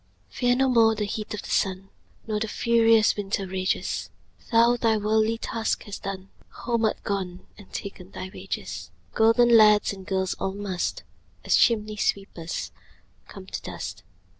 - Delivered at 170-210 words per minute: No, average, 160 wpm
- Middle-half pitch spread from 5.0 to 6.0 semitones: No, average, 2.9 semitones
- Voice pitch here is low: No, high, 210 Hz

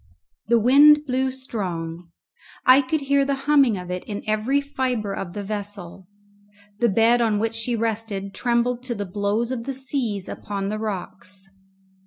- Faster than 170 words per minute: No, average, 165 wpm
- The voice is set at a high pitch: Yes, high, 225 Hz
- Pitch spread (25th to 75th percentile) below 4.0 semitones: No, average, 4.4 semitones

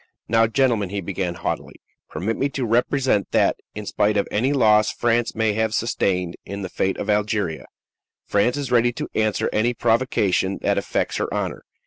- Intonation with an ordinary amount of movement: Yes, average, 3.0 semitones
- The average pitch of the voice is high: No, low, 110 Hz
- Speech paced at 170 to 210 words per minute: Yes, average, 175 wpm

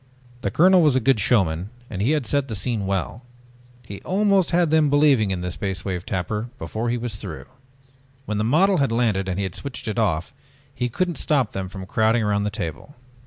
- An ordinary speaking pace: No, fast, 215 wpm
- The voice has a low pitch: Yes, low, 110 Hz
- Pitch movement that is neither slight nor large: No, wide, 6.5 semitones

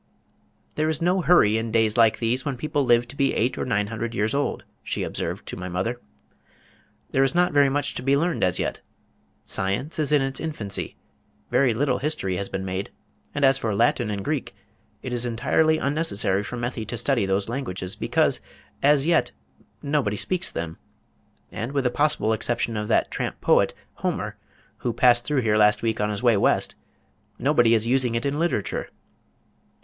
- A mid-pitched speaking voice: No, low, 120 Hz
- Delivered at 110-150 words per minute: No, average, 185 wpm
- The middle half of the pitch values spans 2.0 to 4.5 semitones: No, average, 4.9 semitones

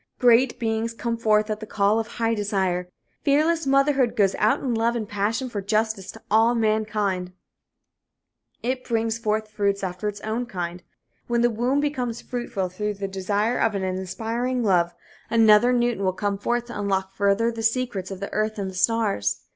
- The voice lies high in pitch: Yes, high, 220 Hz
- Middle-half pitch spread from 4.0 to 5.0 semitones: No, average, 3.0 semitones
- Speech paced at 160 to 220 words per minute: Yes, average, 180 wpm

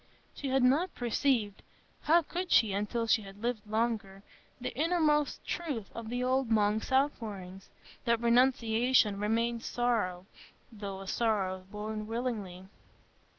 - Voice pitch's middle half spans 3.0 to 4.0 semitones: Yes, average, 3.5 semitones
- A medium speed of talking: No, slow, 125 wpm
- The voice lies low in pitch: No, high, 230 Hz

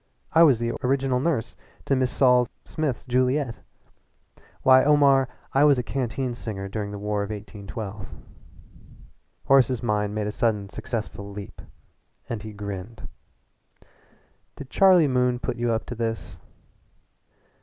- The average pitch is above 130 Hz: No, low, 120 Hz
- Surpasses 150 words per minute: No, slow, 135 wpm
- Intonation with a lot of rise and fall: No, average, 4.0 semitones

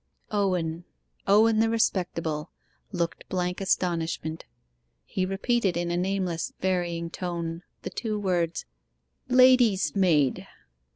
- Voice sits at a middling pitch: Yes, medium, 180 Hz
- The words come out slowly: Yes, slow, 105 wpm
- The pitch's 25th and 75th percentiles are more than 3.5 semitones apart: No, average, 3.1 semitones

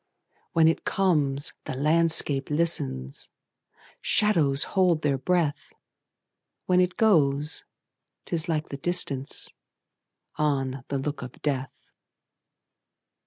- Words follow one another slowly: Yes, slow, 90 wpm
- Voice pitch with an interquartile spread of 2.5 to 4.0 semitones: Yes, average, 3.6 semitones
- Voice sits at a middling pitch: Yes, medium, 150 Hz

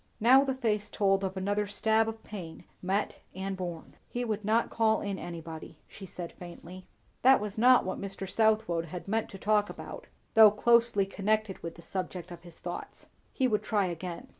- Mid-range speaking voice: No, high, 200 Hz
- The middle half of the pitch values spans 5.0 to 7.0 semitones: No, average, 3.2 semitones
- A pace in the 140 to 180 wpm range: No, average, 190 wpm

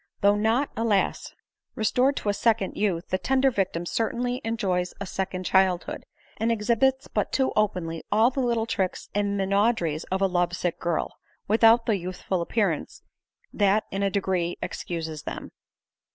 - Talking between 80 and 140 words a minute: No, average, 155 wpm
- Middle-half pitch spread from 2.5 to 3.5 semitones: No, average, 3.9 semitones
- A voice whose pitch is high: Yes, high, 200 Hz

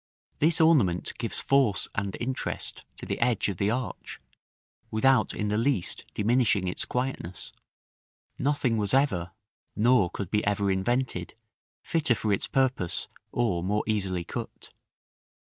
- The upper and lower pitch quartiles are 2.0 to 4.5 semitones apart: No, average, 5.2 semitones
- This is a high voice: No, low, 110 Hz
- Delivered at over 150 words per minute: No, slow, 135 wpm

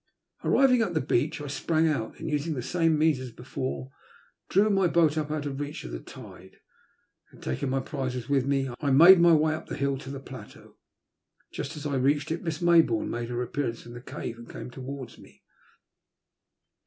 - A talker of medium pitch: Yes, medium, 145 Hz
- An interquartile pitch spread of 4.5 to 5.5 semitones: No, average, 3.9 semitones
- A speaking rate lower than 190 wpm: No, fast, 205 wpm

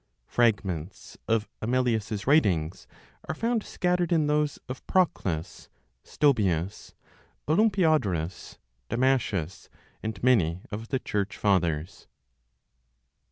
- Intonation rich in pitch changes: Yes, wide, 8.1 semitones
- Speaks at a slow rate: Yes, slow, 90 wpm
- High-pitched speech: No, low, 110 Hz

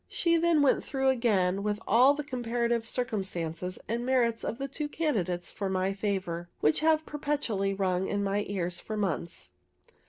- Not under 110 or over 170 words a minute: Yes, average, 165 wpm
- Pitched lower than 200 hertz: No, high, 215 Hz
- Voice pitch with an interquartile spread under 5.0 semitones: No, wide, 5.6 semitones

